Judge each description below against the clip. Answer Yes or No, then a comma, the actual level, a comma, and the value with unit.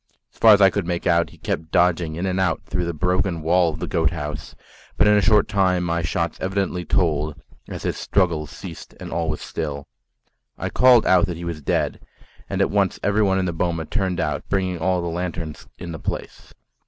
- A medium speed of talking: No, fast, 215 wpm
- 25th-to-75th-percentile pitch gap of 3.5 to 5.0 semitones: No, narrow, 2.5 semitones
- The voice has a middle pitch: No, very low, 85 Hz